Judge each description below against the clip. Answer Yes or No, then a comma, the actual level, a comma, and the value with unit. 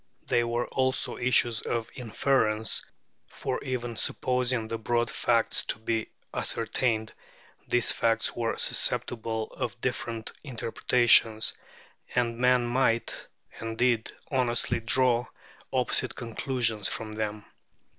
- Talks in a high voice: No, low, 120 Hz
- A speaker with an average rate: No, slow, 110 wpm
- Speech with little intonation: Yes, narrow, 1.7 semitones